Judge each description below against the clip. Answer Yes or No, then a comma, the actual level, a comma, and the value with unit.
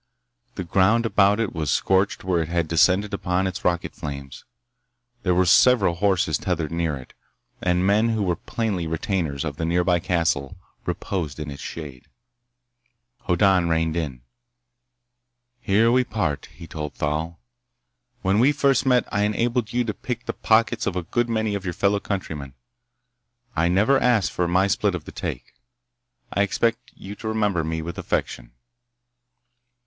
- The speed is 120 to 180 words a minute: Yes, average, 160 wpm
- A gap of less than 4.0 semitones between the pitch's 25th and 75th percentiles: No, average, 4.4 semitones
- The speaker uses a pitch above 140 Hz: No, very low, 90 Hz